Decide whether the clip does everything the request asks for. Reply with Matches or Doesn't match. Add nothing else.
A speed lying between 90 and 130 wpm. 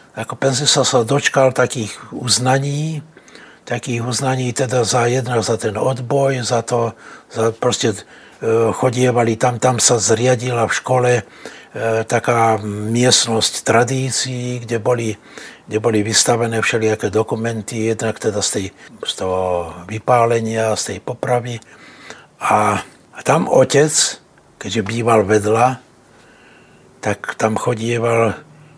Matches